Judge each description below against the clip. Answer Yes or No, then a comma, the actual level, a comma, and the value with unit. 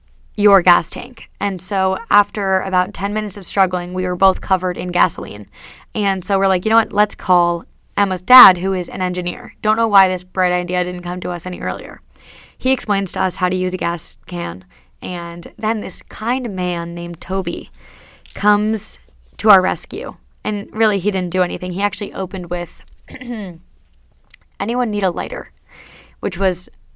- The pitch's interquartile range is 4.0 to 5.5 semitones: No, narrow, 2.5 semitones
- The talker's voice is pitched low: No, medium, 185 Hz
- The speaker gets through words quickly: No, average, 180 wpm